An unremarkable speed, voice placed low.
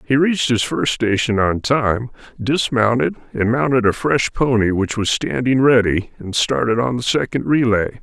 Yes: average, 170 wpm; low, 120 Hz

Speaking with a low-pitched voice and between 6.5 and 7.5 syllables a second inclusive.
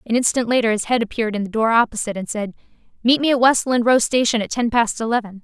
No: high, 230 Hz; 6.9 syllables/s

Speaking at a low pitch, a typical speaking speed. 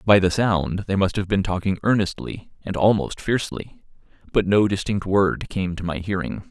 Yes: very low, 95 Hz; average, 185 wpm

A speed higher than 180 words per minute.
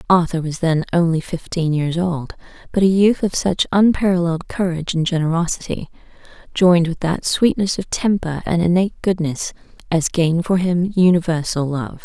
No: average, 155 wpm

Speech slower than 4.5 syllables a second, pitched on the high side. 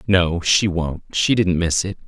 No: 3.8 syllables/s; very low, 90 Hz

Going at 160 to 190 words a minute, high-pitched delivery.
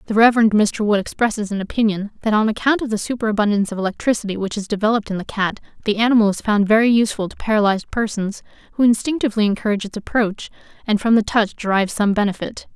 No: average, 200 wpm; high, 215 Hz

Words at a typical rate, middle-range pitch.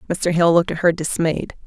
No: fast, 215 wpm; medium, 170 Hz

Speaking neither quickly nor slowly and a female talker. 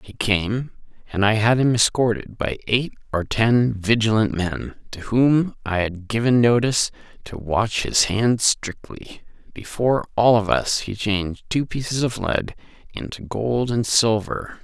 No: average, 155 wpm; male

